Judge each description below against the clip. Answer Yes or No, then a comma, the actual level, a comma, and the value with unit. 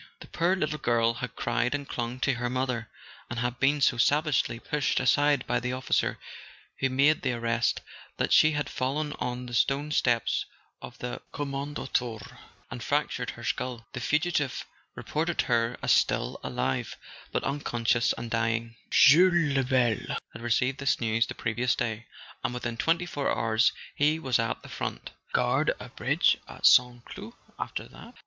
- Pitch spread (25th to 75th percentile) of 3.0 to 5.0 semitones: Yes, average, 3.5 semitones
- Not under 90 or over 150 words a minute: No, average, 170 wpm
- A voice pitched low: Yes, low, 125 Hz